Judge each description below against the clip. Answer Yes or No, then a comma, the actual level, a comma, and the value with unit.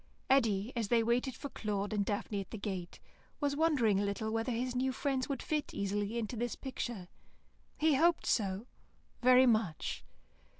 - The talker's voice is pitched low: No, high, 230 Hz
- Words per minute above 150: Yes, average, 170 wpm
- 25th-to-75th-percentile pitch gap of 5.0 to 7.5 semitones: No, average, 4.3 semitones